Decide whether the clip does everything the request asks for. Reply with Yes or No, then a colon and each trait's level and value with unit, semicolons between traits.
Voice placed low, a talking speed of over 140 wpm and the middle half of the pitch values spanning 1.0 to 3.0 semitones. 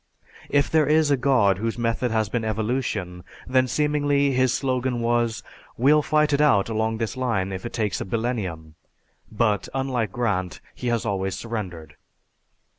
No: low, 115 Hz; average, 160 wpm; average, 4.1 semitones